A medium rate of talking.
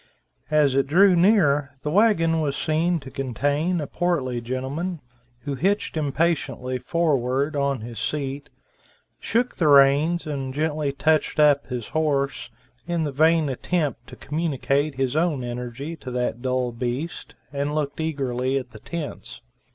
Yes: average, 145 wpm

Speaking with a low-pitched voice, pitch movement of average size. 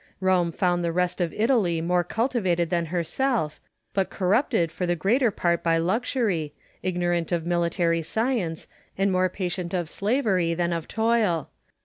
No: medium, 180 Hz; average, 3.2 semitones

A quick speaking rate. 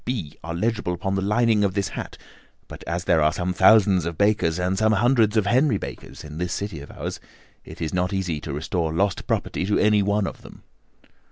Yes: fast, 215 wpm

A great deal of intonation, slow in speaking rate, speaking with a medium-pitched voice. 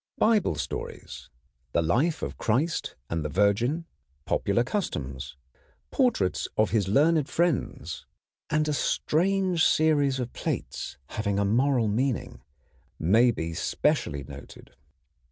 No: wide, 8.1 semitones; slow, 120 wpm; low, 120 Hz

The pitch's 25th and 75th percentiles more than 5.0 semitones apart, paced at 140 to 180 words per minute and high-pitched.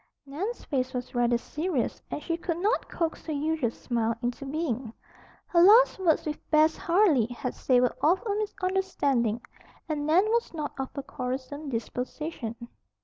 Yes: wide, 5.4 semitones; average, 155 wpm; very high, 295 Hz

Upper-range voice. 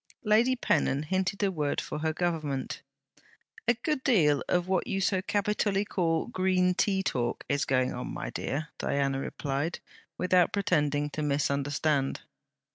No: medium, 165 Hz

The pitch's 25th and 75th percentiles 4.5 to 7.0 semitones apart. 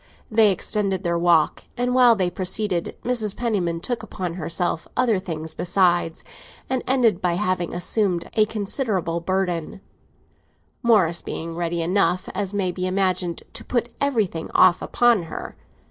No: average, 3.9 semitones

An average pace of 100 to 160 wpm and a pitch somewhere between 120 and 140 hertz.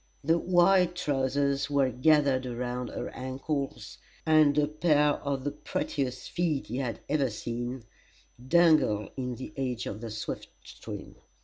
Yes: average, 140 wpm; low, 135 Hz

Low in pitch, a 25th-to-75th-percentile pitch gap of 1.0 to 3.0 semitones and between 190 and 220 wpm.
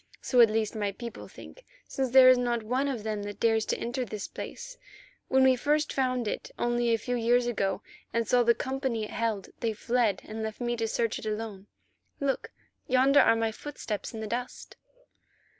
No: high, 235 Hz; narrow, 2.6 semitones; average, 200 wpm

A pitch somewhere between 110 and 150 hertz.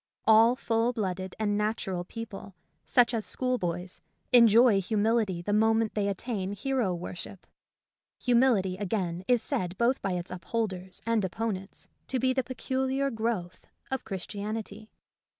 No: high, 215 Hz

